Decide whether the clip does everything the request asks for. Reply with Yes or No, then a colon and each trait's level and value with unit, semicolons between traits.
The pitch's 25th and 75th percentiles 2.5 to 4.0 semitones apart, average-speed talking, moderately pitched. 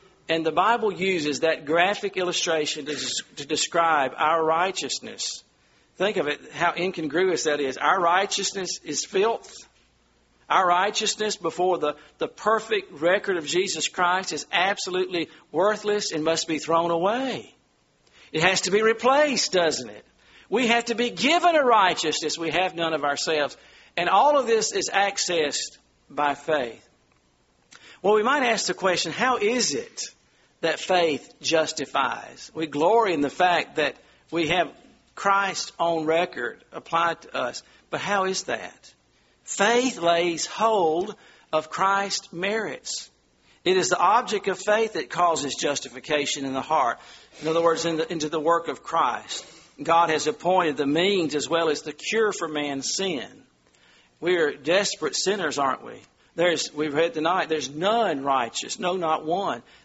No: average, 4.7 semitones; average, 155 wpm; medium, 170 Hz